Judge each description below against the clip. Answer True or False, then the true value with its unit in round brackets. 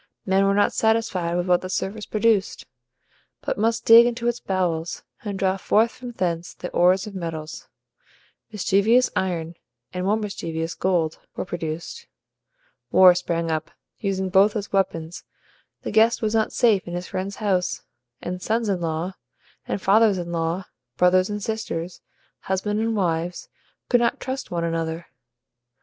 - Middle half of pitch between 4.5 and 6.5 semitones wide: False (3.8 semitones)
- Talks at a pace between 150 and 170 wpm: True (155 wpm)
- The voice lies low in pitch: False (190 Hz)